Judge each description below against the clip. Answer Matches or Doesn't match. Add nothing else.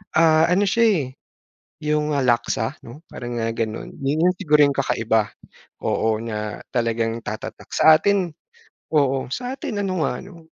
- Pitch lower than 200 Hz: Matches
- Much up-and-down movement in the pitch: Matches